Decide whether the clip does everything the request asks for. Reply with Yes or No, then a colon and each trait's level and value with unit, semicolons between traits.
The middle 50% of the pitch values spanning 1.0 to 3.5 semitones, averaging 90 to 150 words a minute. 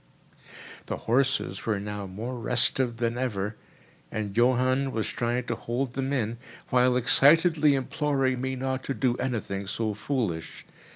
Yes: average, 3.1 semitones; average, 140 wpm